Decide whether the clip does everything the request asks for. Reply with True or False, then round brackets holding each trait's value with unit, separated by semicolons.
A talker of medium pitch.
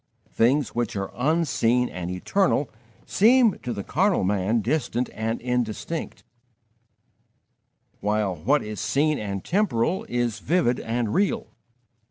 False (120 Hz)